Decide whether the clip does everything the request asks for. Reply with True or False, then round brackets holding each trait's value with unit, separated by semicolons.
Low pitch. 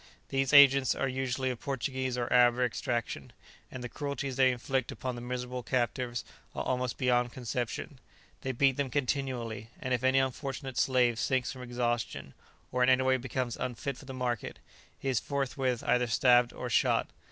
True (125 Hz)